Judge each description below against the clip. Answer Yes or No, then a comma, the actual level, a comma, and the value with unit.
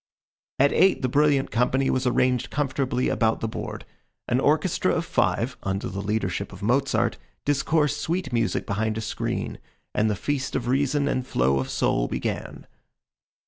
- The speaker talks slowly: No, average, 160 wpm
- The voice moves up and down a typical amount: Yes, average, 4.6 semitones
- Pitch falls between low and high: No, low, 125 Hz